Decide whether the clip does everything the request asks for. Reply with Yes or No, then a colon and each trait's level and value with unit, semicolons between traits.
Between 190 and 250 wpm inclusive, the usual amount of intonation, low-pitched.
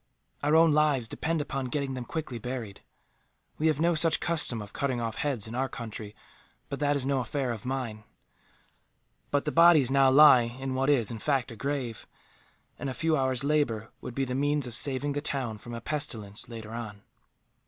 Yes: average, 195 wpm; average, 3.8 semitones; low, 130 Hz